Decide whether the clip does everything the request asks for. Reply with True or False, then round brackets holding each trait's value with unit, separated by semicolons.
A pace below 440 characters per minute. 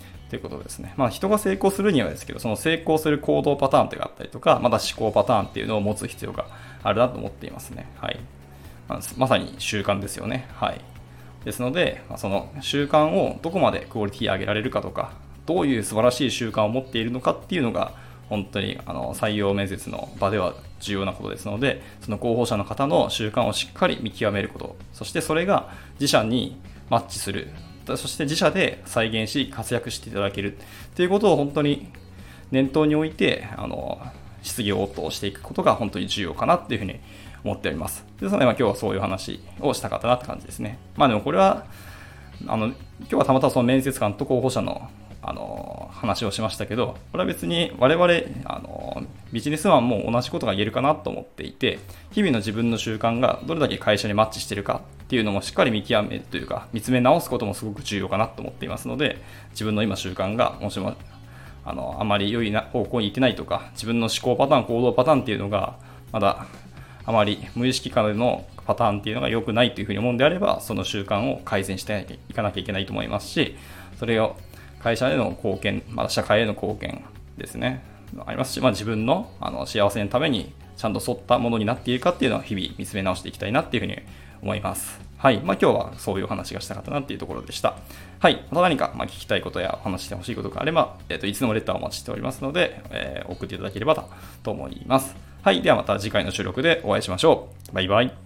False (445 characters per minute)